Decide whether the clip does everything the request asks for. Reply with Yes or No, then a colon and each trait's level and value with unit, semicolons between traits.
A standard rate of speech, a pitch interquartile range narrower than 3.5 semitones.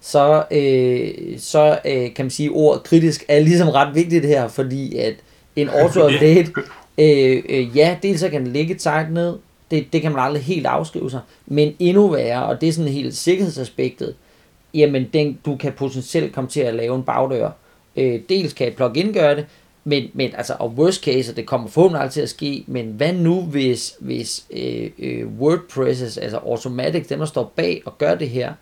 No: average, 195 wpm; average, 3.8 semitones